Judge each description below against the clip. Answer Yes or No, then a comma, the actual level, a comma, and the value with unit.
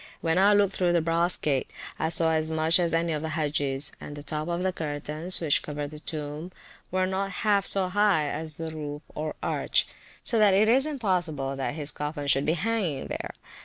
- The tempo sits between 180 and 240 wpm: Yes, fast, 205 wpm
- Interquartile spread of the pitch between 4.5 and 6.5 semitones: No, average, 3.8 semitones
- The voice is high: No, medium, 160 Hz